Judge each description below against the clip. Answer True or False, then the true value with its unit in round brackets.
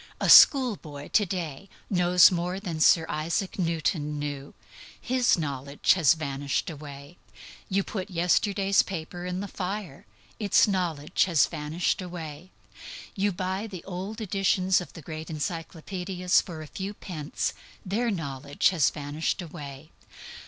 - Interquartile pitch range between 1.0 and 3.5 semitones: False (4.0 semitones)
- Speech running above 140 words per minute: False (135 wpm)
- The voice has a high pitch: False (175 Hz)